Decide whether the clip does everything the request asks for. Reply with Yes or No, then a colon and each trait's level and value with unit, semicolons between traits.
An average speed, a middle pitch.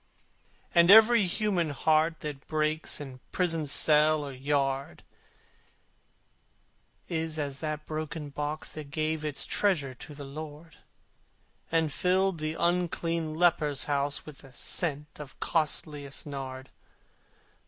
No: slow, 120 wpm; medium, 155 Hz